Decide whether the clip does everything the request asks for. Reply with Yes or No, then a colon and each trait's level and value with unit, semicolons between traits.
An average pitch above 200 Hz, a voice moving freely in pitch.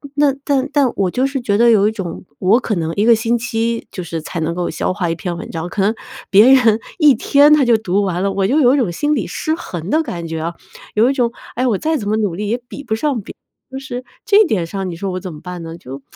Yes: high, 210 Hz; wide, 6.0 semitones